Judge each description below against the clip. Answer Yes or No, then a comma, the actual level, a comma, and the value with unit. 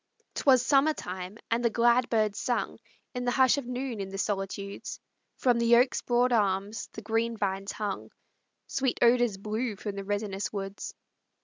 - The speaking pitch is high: Yes, high, 225 Hz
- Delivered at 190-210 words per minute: No, average, 170 wpm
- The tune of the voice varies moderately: Yes, average, 3.5 semitones